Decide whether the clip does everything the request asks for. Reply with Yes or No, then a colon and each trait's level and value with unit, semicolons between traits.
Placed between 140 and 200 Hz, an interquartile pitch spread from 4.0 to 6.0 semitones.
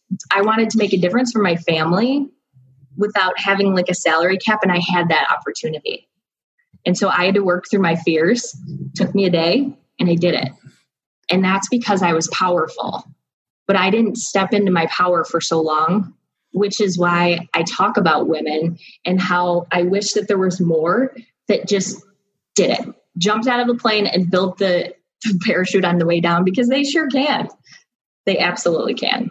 No: medium, 185 Hz; average, 3.6 semitones